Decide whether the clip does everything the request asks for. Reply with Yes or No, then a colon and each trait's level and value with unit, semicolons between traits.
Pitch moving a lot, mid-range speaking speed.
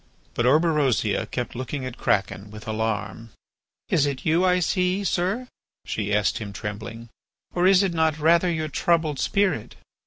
Yes: wide, 7.6 semitones; average, 155 wpm